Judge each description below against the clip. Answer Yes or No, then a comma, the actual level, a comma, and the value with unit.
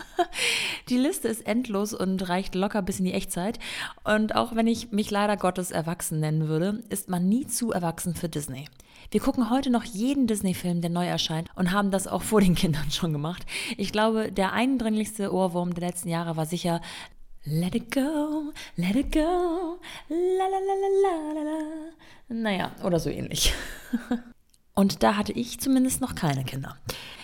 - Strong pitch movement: Yes, wide, 6.2 semitones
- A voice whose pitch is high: Yes, high, 205 Hz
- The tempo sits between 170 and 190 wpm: Yes, average, 175 wpm